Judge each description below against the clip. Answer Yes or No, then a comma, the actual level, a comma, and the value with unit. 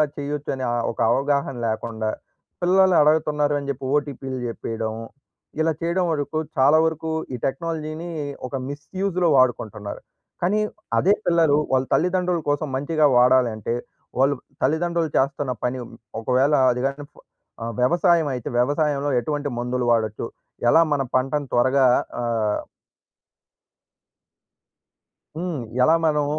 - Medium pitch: Yes, medium, 145 Hz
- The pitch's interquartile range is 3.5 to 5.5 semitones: Yes, average, 4.0 semitones